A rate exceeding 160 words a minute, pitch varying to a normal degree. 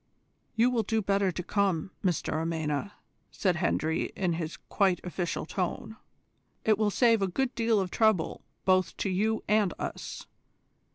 No: average, 155 wpm; average, 3.9 semitones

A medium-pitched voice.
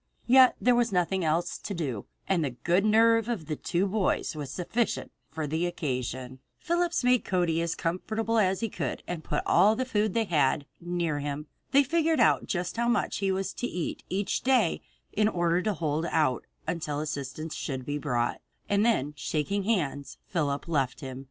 Yes: medium, 175 Hz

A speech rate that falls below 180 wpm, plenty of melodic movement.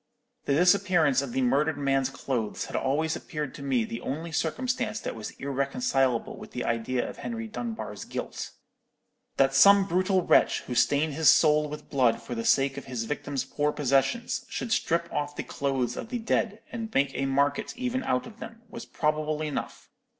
No: average, 185 wpm; wide, 6.5 semitones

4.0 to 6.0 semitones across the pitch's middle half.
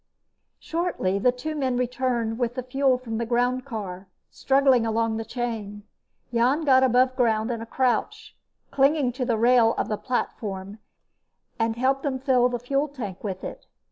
No: narrow, 2.6 semitones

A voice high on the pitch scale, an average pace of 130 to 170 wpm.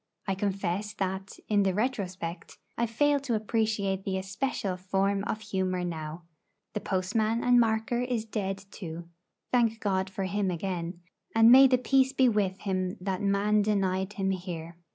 Yes: high, 195 Hz; average, 160 wpm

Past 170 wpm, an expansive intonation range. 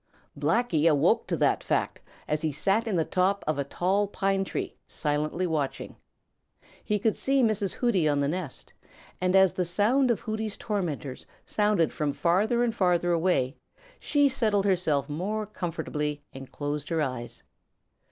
No: average, 160 wpm; wide, 5.7 semitones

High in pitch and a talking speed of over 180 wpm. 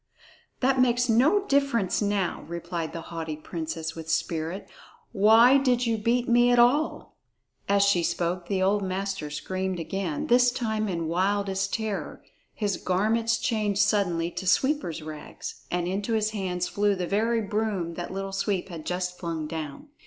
No: high, 195 Hz; average, 160 wpm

